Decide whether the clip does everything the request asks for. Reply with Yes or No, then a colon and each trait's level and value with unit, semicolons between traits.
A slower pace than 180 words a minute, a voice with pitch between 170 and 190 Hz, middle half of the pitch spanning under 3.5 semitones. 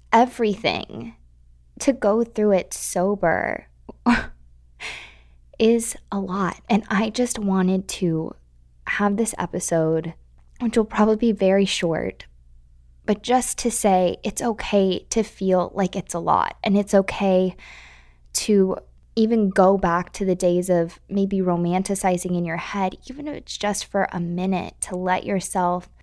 No: average, 140 wpm; medium, 185 Hz; average, 3.8 semitones